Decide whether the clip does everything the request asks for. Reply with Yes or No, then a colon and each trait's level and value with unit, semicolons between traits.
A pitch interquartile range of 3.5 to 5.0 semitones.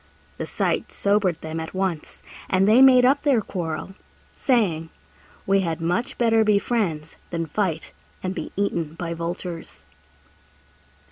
Yes: average, 4.5 semitones